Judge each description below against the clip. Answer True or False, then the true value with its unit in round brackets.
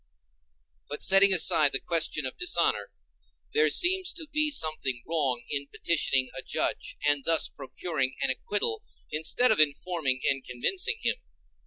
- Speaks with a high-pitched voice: False (155 Hz)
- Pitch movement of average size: False (5.9 semitones)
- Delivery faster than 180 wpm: False (145 wpm)